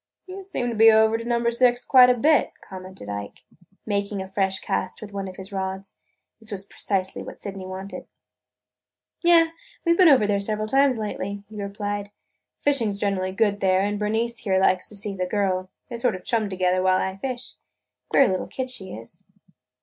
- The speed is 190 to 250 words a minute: Yes, average, 195 wpm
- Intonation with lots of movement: No, average, 3.6 semitones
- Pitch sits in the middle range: No, high, 205 Hz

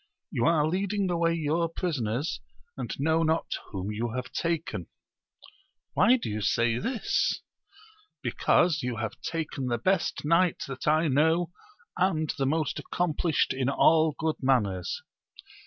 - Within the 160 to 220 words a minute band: No, average, 150 wpm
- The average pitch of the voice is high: No, medium, 155 Hz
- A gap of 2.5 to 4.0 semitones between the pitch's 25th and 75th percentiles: No, average, 4.8 semitones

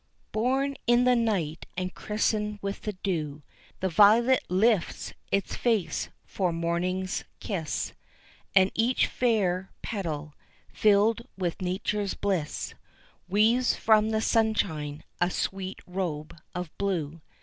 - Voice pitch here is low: No, high, 195 Hz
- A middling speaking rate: No, slow, 115 wpm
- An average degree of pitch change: Yes, average, 3.8 semitones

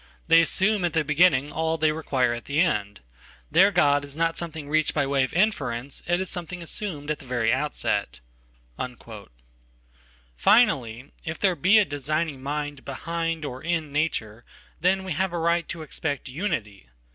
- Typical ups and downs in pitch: Yes, average, 3.7 semitones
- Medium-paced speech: Yes, average, 165 wpm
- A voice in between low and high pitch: Yes, medium, 155 Hz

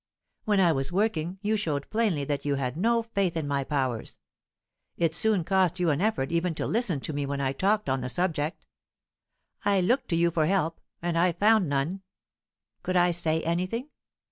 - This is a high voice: No, medium, 170 Hz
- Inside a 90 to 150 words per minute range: No, average, 195 wpm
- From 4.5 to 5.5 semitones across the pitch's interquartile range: Yes, average, 5.1 semitones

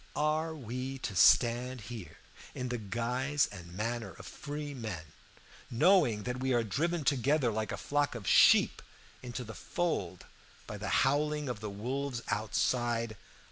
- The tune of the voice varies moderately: Yes, average, 4.4 semitones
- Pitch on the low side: Yes, low, 125 Hz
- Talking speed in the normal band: Yes, average, 150 wpm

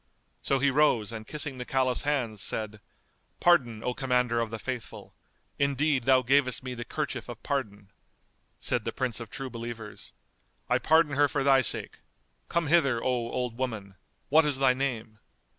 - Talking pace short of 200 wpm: Yes, average, 170 wpm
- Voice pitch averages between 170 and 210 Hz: No, low, 130 Hz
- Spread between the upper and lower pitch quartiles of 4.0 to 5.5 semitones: No, average, 3.2 semitones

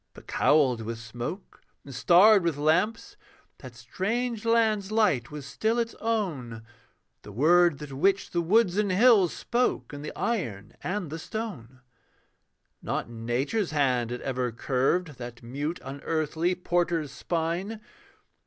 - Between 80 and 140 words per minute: Yes, slow, 135 wpm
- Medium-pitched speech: Yes, medium, 160 Hz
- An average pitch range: No, wide, 8.2 semitones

